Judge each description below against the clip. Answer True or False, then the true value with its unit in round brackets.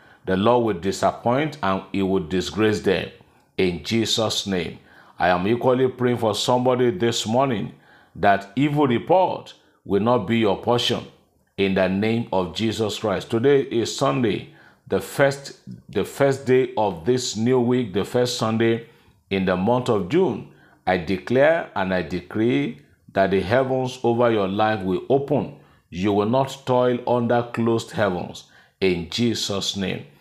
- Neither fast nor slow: True (155 wpm)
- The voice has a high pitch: False (115 Hz)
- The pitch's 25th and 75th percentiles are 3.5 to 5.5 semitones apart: True (4.2 semitones)